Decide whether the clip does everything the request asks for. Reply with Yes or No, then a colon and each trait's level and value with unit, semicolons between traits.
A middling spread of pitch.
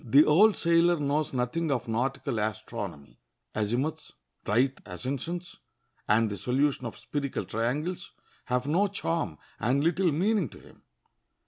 No: wide, 6.2 semitones